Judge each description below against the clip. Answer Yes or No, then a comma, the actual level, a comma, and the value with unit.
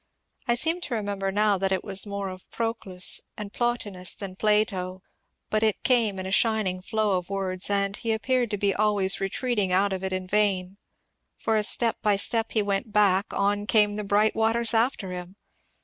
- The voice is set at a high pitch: Yes, high, 205 Hz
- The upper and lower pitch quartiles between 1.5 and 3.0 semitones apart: Yes, narrow, 2.4 semitones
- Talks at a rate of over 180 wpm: Yes, average, 190 wpm